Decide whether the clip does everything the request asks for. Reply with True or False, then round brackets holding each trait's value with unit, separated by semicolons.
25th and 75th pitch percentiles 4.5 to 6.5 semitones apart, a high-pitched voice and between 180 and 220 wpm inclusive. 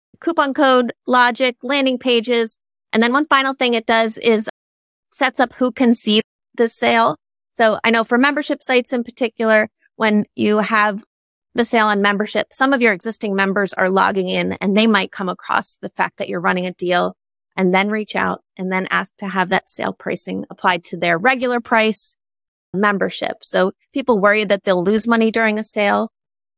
False (3.5 semitones; 225 Hz; 185 wpm)